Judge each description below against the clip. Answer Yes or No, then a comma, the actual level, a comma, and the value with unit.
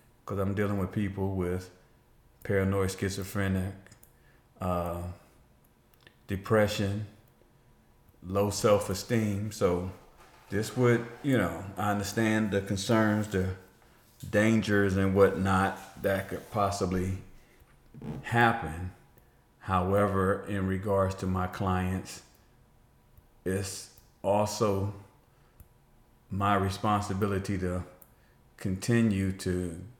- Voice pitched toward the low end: Yes, low, 100 Hz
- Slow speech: Yes, slow, 85 wpm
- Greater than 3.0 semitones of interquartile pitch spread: No, narrow, 2.4 semitones